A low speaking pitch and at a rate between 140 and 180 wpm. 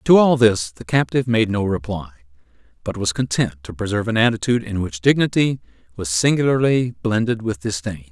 Yes: low, 110 Hz; average, 170 wpm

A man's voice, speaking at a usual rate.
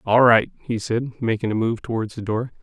No: male; fast, 230 wpm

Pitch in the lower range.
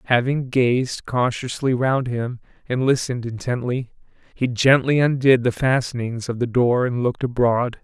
Yes: low, 125 Hz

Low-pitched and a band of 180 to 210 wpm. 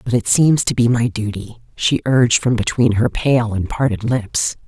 Yes: low, 115 Hz; fast, 205 wpm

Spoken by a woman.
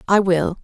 Yes: female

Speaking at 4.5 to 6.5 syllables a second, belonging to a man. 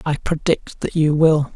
No: 4.1 syllables/s; male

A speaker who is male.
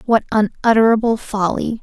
No: female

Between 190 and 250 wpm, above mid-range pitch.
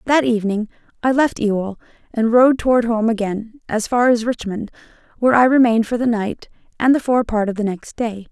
Yes: average, 195 wpm; high, 230 Hz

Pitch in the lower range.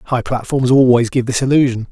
Yes: low, 125 Hz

